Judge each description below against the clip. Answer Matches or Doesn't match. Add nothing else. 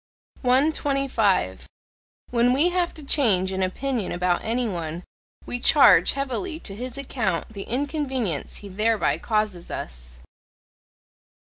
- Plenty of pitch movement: Matches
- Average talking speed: Doesn't match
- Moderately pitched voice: Doesn't match